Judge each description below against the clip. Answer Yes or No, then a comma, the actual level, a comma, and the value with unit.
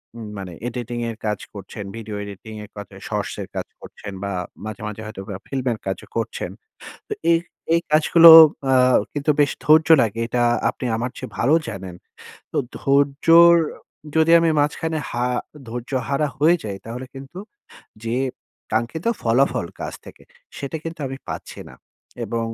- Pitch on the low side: Yes, low, 125 Hz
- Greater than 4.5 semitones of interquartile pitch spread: Yes, average, 5.3 semitones